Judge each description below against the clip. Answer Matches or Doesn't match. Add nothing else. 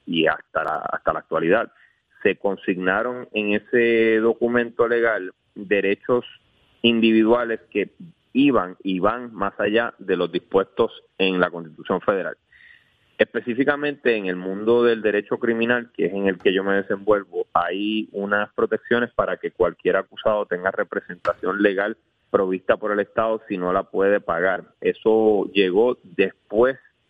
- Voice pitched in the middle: Doesn't match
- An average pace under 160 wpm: Matches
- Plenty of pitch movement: Doesn't match